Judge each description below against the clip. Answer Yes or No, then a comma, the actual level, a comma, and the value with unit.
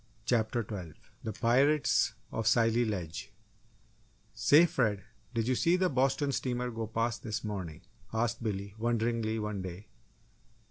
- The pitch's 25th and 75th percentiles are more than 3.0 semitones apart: No, narrow, 2.6 semitones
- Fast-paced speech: No, slow, 135 wpm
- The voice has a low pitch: Yes, low, 115 Hz